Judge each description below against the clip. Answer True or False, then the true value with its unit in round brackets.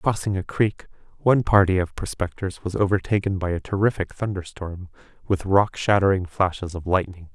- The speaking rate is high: False (155 wpm)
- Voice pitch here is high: False (95 Hz)